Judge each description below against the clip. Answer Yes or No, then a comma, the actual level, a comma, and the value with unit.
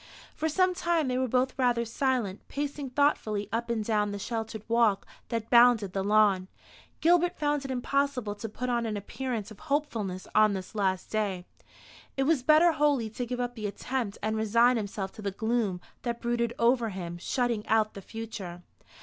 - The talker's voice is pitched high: Yes, high, 230 Hz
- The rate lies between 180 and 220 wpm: Yes, average, 185 wpm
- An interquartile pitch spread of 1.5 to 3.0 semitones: No, average, 3.8 semitones